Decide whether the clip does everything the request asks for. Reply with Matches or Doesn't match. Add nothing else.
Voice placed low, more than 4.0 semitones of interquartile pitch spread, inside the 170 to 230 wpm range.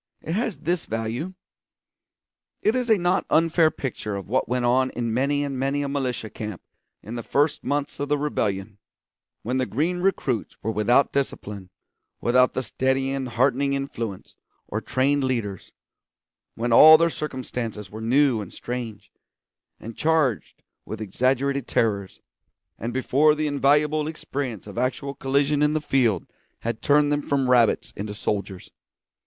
Doesn't match